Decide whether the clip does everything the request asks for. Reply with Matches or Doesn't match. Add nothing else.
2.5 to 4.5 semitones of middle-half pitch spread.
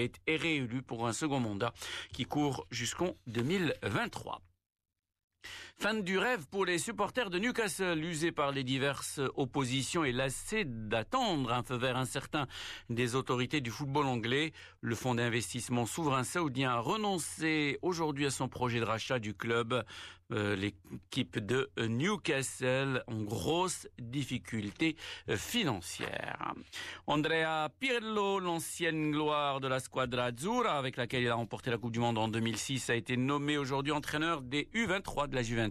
Doesn't match